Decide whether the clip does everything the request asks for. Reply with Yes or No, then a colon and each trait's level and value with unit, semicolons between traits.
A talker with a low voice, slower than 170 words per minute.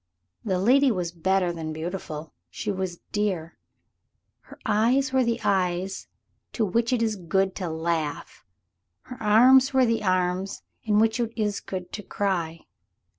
No: high, 195 Hz; average, 150 wpm